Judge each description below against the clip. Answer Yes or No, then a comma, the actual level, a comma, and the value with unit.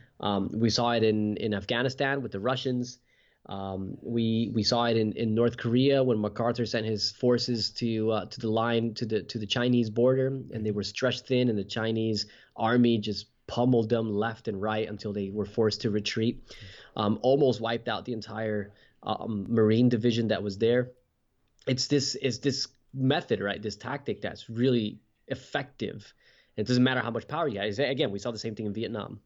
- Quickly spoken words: No, average, 195 wpm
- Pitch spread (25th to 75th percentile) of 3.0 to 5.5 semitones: No, narrow, 2.5 semitones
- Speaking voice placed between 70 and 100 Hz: No, low, 115 Hz